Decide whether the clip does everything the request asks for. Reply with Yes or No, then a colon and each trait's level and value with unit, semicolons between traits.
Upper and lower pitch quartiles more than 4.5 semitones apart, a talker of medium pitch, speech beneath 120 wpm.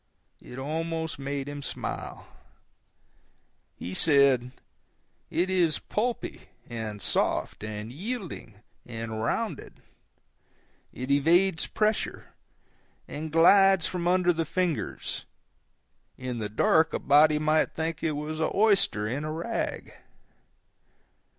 Yes: wide, 5.4 semitones; medium, 155 Hz; slow, 110 wpm